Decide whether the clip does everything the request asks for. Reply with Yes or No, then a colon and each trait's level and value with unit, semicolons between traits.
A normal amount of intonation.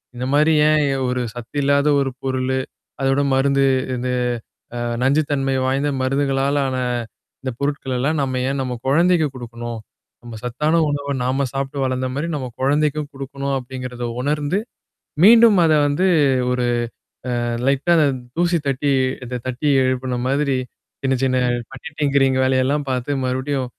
No: narrow, 2.0 semitones